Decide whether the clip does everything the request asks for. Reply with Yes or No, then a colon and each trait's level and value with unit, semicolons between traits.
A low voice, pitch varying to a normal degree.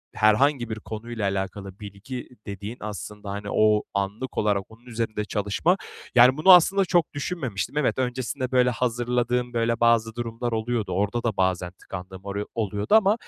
Yes: low, 115 Hz; average, 3.4 semitones